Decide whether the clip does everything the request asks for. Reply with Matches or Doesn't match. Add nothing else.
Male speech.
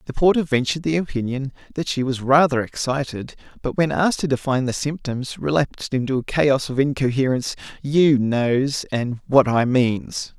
Matches